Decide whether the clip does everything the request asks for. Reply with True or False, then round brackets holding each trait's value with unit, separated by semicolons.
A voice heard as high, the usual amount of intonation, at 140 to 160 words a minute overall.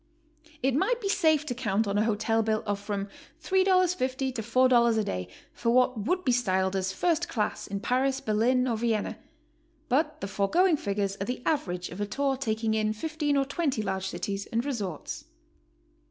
False (235 Hz; 5.0 semitones; 185 wpm)